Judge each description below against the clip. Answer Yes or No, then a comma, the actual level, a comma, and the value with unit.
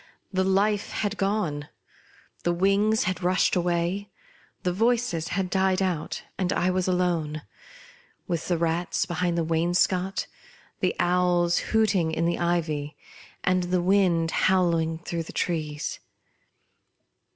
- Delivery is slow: Yes, slow, 130 wpm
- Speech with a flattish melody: Yes, narrow, 2.2 semitones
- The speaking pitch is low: No, medium, 180 Hz